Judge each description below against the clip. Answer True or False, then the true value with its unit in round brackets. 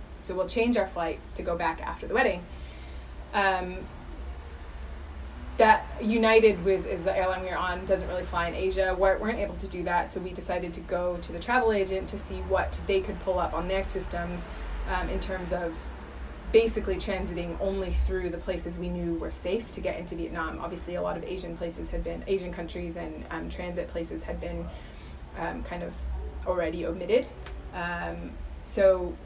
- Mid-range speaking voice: True (175 Hz)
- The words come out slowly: False (190 wpm)